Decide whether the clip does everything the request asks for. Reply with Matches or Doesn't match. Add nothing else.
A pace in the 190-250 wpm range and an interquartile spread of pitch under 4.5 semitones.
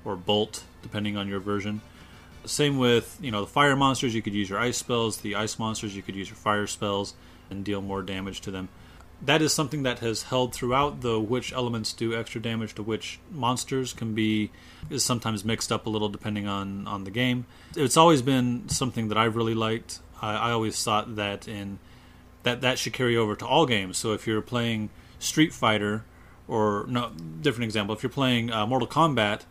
Matches